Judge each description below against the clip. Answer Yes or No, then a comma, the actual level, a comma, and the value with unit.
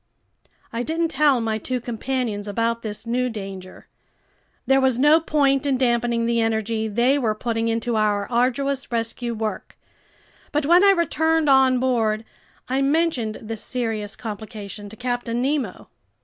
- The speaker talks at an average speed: Yes, average, 150 wpm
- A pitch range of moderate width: Yes, average, 3.5 semitones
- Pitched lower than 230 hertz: No, high, 240 Hz